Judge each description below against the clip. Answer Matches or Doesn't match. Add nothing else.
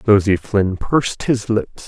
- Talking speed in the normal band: Matches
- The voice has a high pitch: Doesn't match